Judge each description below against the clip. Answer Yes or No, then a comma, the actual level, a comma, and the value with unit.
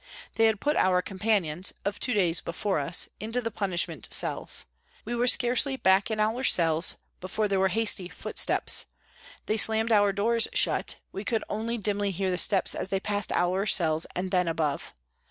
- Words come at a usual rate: Yes, average, 185 wpm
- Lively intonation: No, average, 3.5 semitones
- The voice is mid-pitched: No, high, 200 Hz